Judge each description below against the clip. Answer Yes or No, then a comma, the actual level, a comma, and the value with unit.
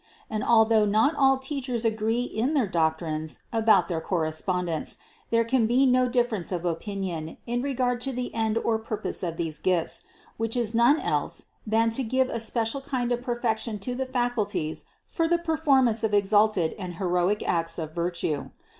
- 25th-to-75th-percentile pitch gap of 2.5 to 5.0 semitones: No, wide, 5.4 semitones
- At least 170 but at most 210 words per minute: Yes, average, 175 wpm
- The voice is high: Yes, high, 225 Hz